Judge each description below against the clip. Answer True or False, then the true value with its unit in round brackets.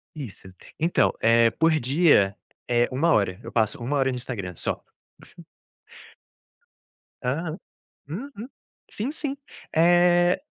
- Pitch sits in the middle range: True (145 Hz)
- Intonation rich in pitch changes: True (7.0 semitones)